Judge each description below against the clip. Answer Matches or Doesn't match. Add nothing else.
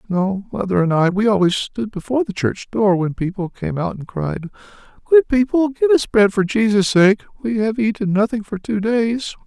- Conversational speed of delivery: Matches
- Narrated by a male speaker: Matches